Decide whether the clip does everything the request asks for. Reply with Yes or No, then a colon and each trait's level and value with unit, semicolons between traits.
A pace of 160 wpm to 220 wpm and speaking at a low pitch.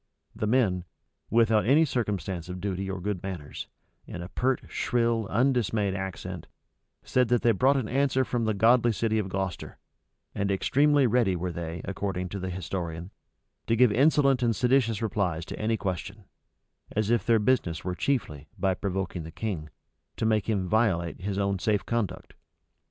Yes: average, 170 wpm; low, 105 Hz